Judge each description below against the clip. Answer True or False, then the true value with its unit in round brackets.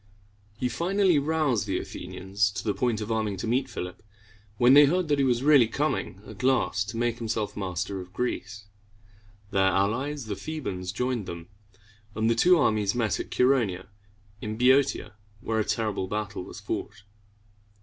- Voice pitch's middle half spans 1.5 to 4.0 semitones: False (4.7 semitones)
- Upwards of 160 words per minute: True (175 wpm)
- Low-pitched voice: True (110 Hz)